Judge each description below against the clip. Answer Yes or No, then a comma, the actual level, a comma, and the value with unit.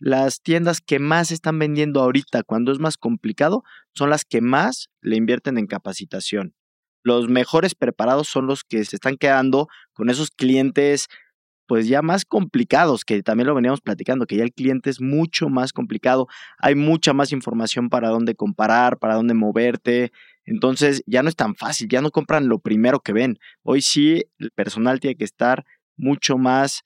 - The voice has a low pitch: Yes, low, 130 Hz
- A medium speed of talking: Yes, average, 180 wpm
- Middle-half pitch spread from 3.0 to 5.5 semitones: Yes, average, 3.7 semitones